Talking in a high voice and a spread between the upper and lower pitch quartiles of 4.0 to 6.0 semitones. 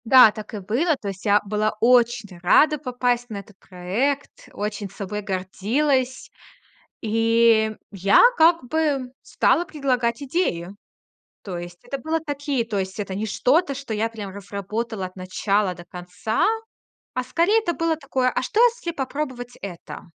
Yes: high, 230 Hz; wide, 5.6 semitones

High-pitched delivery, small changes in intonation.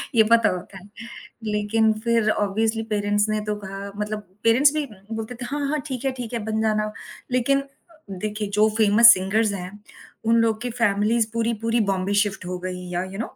Yes: high, 215 Hz; narrow, 2.1 semitones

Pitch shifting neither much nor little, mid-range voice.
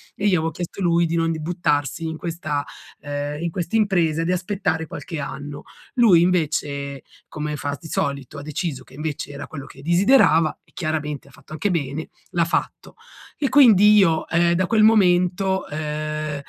Yes: average, 3.3 semitones; medium, 160 Hz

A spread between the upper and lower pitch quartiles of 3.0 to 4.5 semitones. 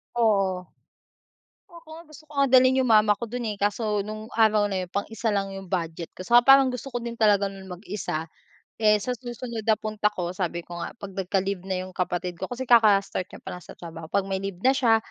Yes: average, 3.9 semitones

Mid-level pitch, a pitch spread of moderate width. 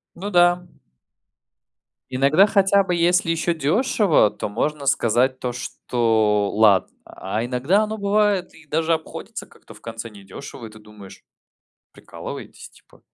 No: medium, 145 Hz; wide, 8.0 semitones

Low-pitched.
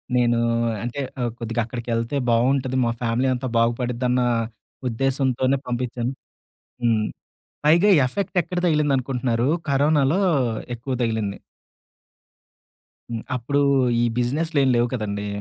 Yes: low, 125 Hz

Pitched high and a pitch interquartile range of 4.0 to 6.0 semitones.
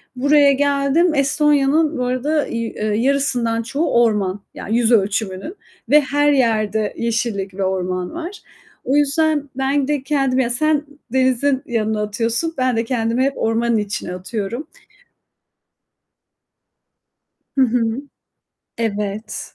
Yes: very high, 250 Hz; average, 4.5 semitones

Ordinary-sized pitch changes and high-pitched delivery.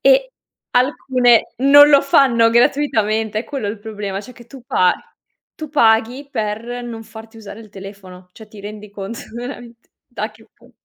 Yes: average, 3.4 semitones; high, 230 Hz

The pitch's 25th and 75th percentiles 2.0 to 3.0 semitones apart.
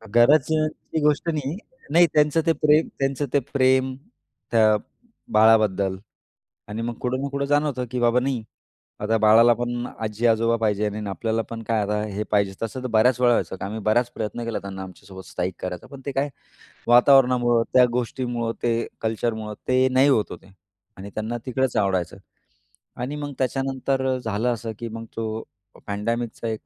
No: average, 3.4 semitones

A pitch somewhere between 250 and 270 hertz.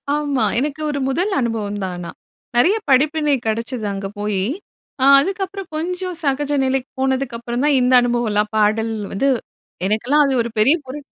Yes: very high, 260 Hz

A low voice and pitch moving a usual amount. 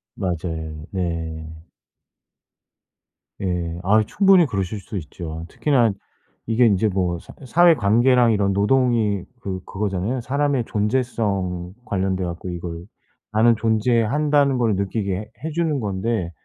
Yes: low, 105 Hz; average, 4.8 semitones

